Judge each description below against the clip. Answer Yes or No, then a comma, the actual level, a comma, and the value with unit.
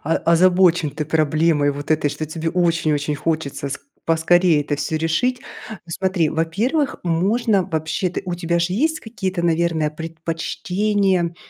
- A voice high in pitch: No, medium, 165 Hz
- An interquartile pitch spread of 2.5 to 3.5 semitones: Yes, average, 2.8 semitones